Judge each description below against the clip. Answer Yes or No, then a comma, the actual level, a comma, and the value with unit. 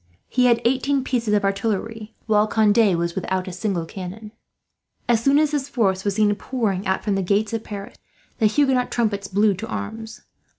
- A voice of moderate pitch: No, high, 215 Hz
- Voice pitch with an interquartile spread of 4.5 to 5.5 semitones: No, average, 3.0 semitones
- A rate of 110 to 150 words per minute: No, average, 185 wpm